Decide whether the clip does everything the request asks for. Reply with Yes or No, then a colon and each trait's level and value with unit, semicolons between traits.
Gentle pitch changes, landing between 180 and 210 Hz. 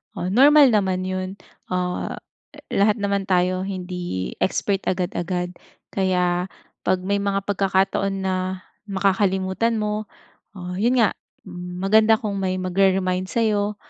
Yes: narrow, 1.8 semitones; high, 190 Hz